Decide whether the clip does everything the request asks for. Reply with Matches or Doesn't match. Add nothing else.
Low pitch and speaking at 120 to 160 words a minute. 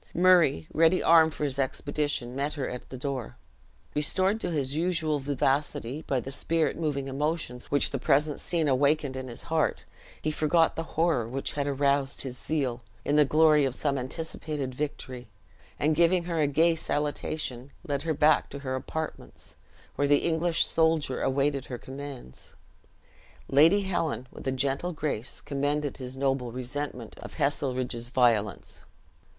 Doesn't match